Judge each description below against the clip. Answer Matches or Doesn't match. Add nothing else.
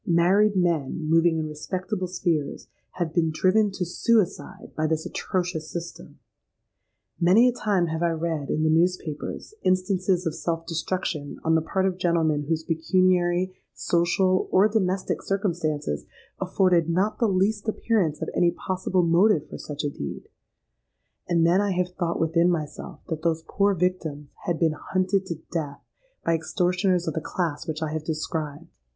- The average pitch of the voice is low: Doesn't match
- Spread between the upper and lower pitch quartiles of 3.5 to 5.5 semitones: Doesn't match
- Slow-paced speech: Doesn't match